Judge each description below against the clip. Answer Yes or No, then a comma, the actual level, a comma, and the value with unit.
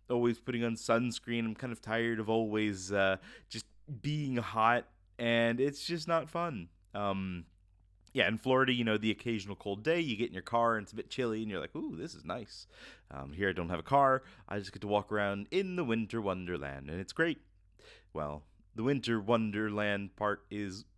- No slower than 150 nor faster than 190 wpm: No, fast, 205 wpm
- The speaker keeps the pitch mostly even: No, average, 3.7 semitones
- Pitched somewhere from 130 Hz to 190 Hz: No, low, 110 Hz